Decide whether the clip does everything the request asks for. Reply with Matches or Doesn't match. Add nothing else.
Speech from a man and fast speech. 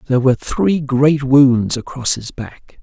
Doesn't match